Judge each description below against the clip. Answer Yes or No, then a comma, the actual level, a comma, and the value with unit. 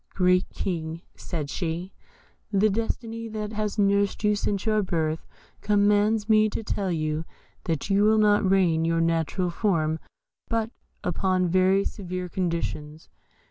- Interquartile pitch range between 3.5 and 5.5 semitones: Yes, average, 3.9 semitones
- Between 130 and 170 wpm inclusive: Yes, average, 140 wpm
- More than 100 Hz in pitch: Yes, high, 190 Hz